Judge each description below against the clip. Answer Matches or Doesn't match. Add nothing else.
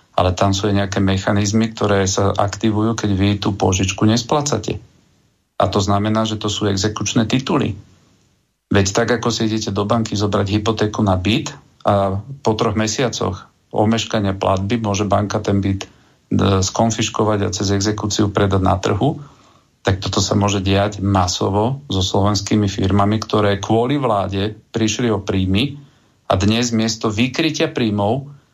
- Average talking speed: Matches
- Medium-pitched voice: Doesn't match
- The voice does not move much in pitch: Matches